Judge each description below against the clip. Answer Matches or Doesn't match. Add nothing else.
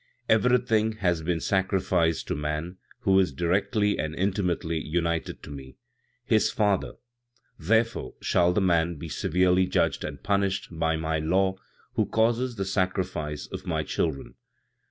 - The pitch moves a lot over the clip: Doesn't match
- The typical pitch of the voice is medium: Doesn't match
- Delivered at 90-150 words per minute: Matches